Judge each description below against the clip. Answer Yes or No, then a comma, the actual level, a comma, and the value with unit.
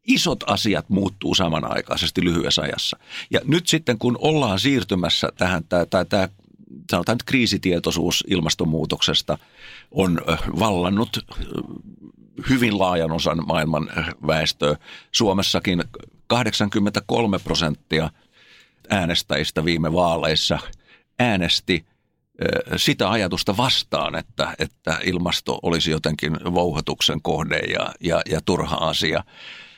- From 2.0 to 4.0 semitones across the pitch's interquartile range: No, average, 4.9 semitones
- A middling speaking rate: No, slow, 90 wpm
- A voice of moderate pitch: No, very low, 90 Hz